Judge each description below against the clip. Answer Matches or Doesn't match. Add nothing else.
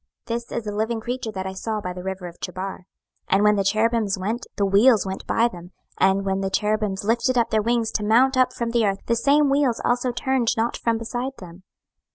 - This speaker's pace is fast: Matches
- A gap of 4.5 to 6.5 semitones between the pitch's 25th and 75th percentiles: Doesn't match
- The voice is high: Matches